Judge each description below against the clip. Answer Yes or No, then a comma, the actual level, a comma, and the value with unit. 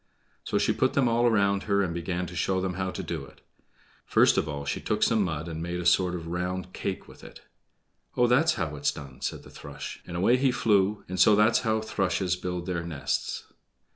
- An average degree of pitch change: Yes, average, 3.6 semitones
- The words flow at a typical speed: No, fast, 225 wpm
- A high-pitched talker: No, very low, 90 Hz